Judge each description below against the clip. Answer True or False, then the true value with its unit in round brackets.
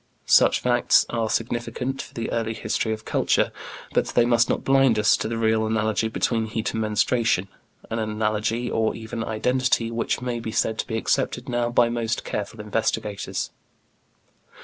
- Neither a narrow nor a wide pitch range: False (1.4 semitones)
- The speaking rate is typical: True (170 wpm)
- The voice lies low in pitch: True (115 Hz)